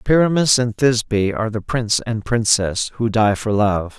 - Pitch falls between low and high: No, low, 115 Hz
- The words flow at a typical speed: Yes, average, 180 wpm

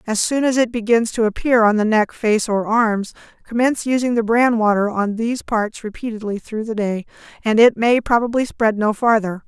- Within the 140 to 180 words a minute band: No, fast, 205 wpm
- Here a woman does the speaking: Yes, female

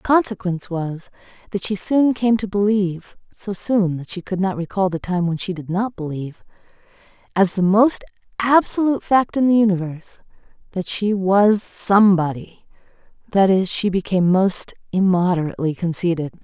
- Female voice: Yes, female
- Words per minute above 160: No, average, 150 wpm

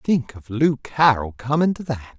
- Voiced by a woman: No, male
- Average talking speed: Yes, average, 190 wpm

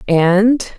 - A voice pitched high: Yes, high, 200 Hz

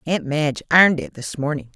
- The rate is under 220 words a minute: Yes, fast, 205 wpm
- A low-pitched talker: No, medium, 150 Hz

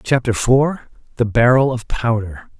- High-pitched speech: No, low, 120 Hz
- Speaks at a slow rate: Yes, slow, 115 wpm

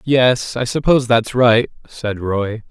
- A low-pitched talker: Yes, low, 120 Hz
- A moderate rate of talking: Yes, average, 155 wpm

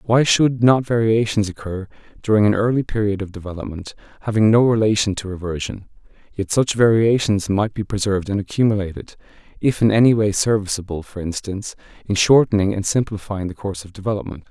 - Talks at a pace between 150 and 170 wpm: Yes, average, 160 wpm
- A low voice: Yes, low, 105 Hz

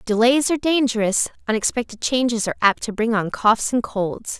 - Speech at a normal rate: Yes, average, 180 wpm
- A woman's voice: Yes, female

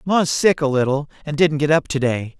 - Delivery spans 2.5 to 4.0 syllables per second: No, 5.1 syllables/s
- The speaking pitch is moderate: Yes, medium, 145 Hz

